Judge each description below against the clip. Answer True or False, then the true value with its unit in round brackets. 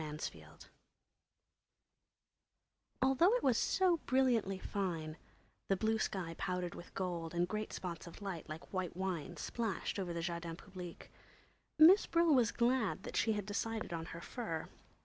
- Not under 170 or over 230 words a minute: False (145 wpm)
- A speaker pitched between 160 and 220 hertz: True (190 Hz)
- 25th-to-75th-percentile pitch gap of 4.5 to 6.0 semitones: True (5.2 semitones)